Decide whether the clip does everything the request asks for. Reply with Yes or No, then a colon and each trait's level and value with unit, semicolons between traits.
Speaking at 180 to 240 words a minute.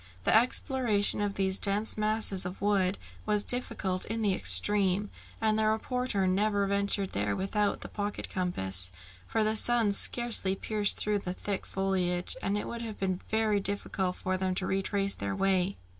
No: average, 170 wpm